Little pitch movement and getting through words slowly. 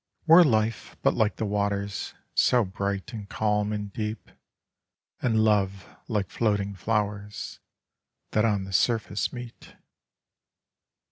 Yes: narrow, 1.6 semitones; slow, 120 wpm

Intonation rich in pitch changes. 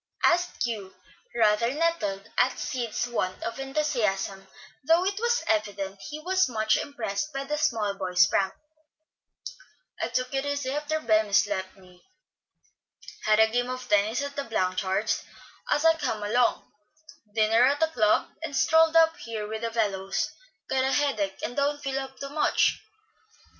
Yes: wide, 5.7 semitones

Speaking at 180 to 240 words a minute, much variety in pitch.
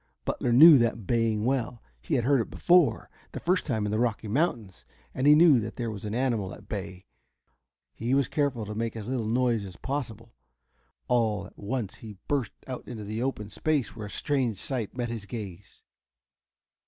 No: average, 190 wpm; average, 3.7 semitones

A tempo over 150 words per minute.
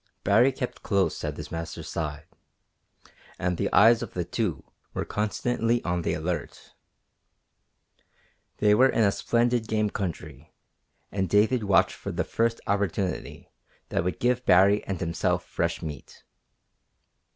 No: average, 140 wpm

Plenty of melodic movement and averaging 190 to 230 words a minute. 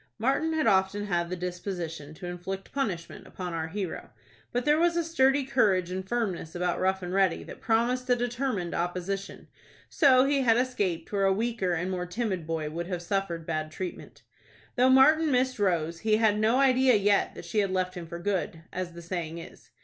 Yes: wide, 5.8 semitones; average, 195 wpm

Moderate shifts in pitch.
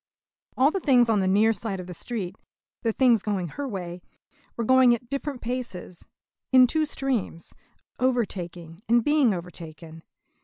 No: wide, 6.0 semitones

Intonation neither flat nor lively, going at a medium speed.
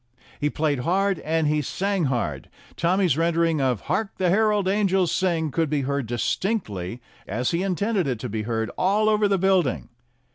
No: wide, 6.6 semitones; average, 175 wpm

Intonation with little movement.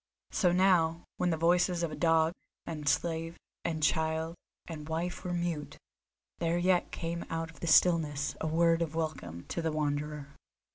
Yes: narrow, 1.6 semitones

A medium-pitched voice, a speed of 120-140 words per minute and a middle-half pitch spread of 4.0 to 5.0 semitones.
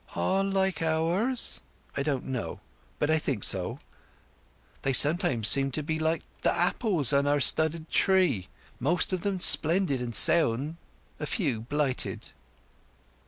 Yes: medium, 155 Hz; slow, 135 wpm; average, 4.5 semitones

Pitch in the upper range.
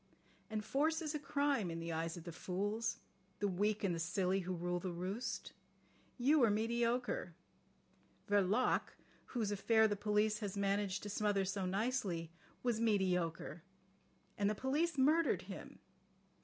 Yes: high, 205 Hz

